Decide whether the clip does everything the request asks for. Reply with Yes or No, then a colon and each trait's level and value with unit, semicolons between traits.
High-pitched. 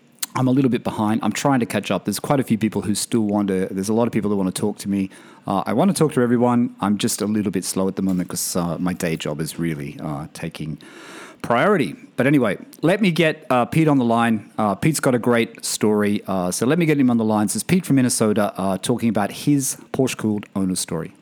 No: low, 110 Hz